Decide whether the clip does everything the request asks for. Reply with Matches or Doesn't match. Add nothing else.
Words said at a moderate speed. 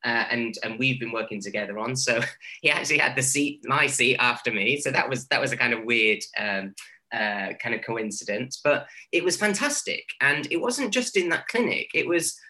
Doesn't match